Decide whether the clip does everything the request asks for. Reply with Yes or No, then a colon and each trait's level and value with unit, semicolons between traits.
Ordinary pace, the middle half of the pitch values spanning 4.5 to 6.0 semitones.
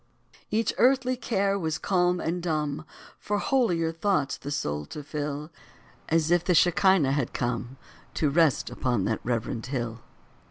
Yes: average, 150 wpm; wide, 5.4 semitones